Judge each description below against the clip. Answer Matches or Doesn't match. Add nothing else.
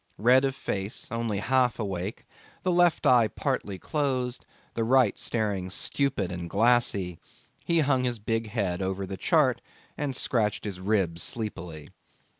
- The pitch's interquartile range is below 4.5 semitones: Doesn't match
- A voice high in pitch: Doesn't match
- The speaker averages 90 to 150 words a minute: Matches